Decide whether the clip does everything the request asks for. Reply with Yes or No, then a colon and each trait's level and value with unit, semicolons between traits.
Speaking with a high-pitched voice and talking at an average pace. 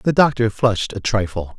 No: low, 110 Hz; average, 190 wpm